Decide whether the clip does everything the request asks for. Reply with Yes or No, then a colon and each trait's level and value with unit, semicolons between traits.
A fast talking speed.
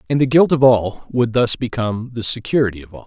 Yes: fast, 235 wpm